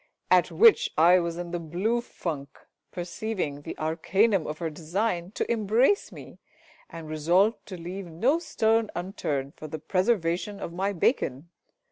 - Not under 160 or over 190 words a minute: No, average, 150 wpm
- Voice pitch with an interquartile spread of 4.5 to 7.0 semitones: Yes, average, 4.9 semitones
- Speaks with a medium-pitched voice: Yes, medium, 175 Hz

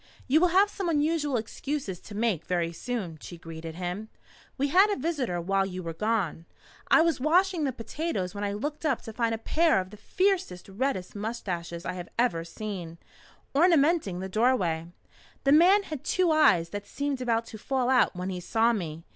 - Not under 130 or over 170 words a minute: No, average, 190 wpm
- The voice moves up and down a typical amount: No, wide, 8.6 semitones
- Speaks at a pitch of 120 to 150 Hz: No, high, 225 Hz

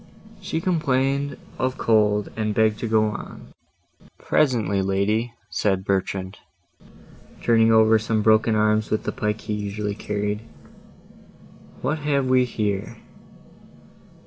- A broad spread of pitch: No, average, 2.8 semitones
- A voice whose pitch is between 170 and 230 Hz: No, low, 110 Hz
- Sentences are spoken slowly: Yes, slow, 120 wpm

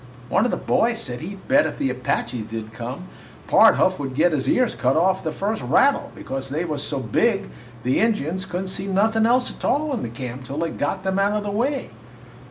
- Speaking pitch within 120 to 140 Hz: No, medium, 185 Hz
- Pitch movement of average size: No, wide, 8.3 semitones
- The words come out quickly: Yes, fast, 230 wpm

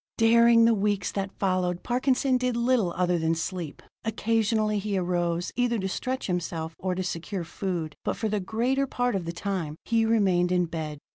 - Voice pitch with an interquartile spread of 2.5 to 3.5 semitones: No, average, 4.5 semitones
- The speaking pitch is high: Yes, high, 195 Hz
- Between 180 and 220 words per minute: Yes, average, 185 wpm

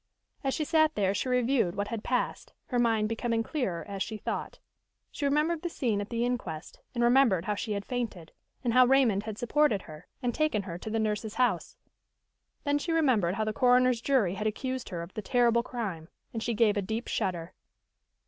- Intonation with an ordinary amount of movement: Yes, average, 3.8 semitones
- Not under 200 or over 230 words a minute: Yes, fast, 205 wpm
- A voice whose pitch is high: Yes, high, 230 Hz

